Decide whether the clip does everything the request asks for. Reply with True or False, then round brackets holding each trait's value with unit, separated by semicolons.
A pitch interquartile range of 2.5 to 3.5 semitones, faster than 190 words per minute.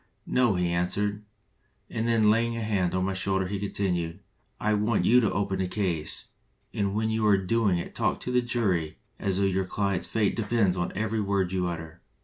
True (2.9 semitones; 200 wpm)